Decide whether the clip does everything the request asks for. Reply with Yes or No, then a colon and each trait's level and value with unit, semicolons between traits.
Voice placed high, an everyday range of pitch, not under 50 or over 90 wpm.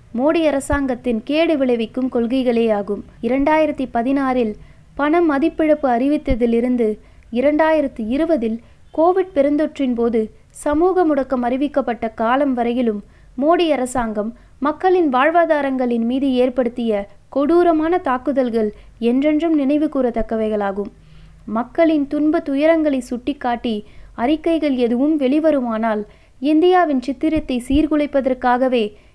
Yes: very high, 265 Hz; average, 4.2 semitones; average, 85 wpm